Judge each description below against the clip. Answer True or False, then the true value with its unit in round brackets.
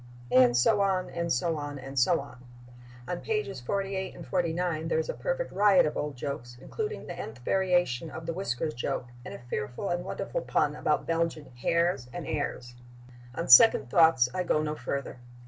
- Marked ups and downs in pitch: True (6.0 semitones)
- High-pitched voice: False (160 Hz)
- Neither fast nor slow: True (185 wpm)